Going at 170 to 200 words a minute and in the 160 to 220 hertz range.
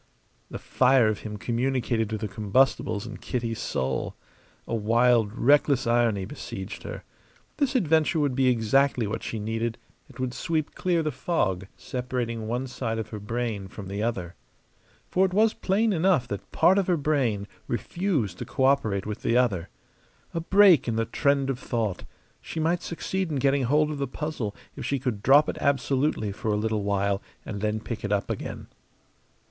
No: average, 180 wpm; low, 120 Hz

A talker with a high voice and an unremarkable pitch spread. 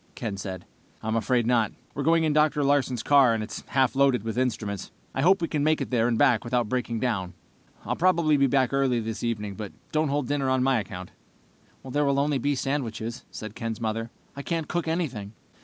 No: low, 130 Hz; average, 4.2 semitones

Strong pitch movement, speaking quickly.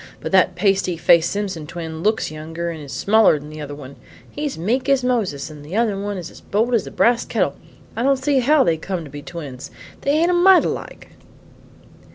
Yes: wide, 7.4 semitones; fast, 215 wpm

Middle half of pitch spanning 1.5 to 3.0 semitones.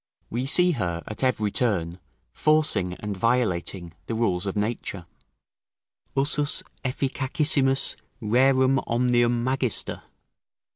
No: average, 4.8 semitones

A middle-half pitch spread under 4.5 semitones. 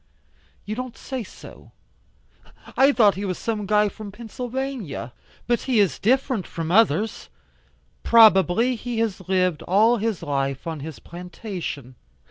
No: average, 4.8 semitones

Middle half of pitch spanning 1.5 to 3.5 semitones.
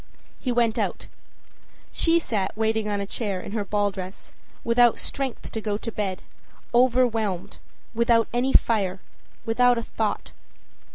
Yes: average, 2.8 semitones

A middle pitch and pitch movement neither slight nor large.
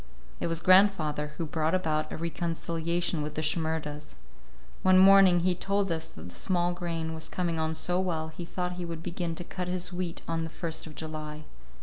No: medium, 165 Hz; narrow, 2.1 semitones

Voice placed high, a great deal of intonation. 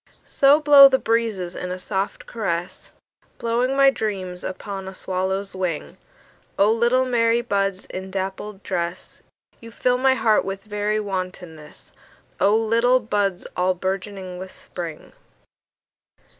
No: high, 200 Hz; average, 3.7 semitones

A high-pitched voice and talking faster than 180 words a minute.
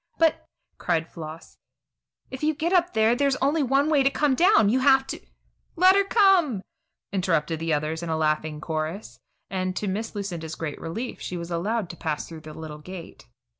Yes: high, 195 Hz; average, 190 wpm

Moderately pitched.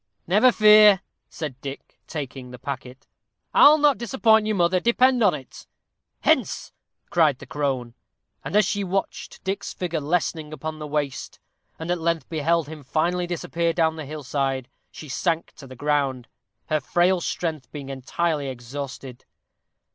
Yes: medium, 160 Hz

